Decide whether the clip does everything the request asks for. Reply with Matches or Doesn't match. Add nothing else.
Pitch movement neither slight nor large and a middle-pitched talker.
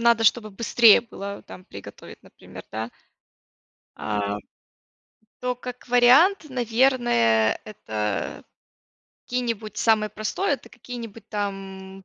Doesn't match